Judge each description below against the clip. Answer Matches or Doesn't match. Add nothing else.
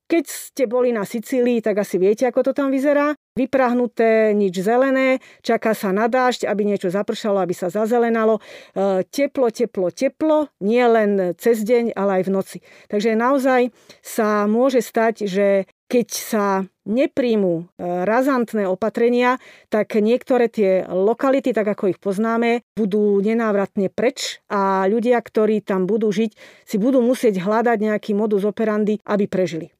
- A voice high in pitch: Matches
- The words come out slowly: Doesn't match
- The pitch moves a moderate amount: Matches